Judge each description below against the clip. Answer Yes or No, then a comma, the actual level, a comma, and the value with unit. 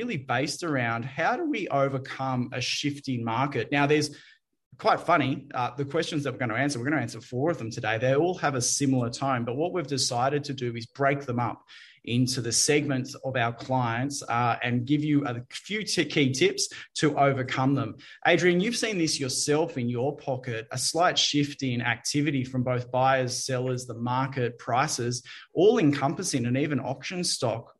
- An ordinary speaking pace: Yes, average, 195 wpm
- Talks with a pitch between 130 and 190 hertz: Yes, low, 135 Hz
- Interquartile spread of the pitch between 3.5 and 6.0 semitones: No, average, 3.0 semitones